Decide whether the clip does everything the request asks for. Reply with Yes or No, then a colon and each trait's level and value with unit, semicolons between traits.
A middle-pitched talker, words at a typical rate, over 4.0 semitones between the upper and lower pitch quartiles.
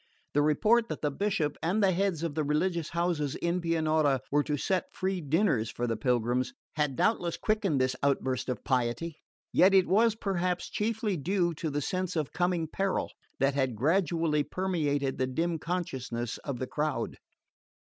Yes: medium, 160 Hz; average, 170 wpm; average, 4.9 semitones